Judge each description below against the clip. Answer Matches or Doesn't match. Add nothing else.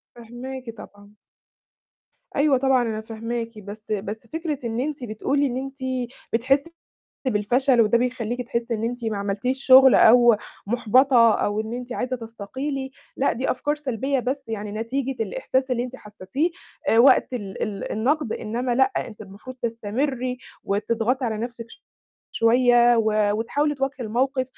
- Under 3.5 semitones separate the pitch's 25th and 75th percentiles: Matches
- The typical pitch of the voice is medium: Doesn't match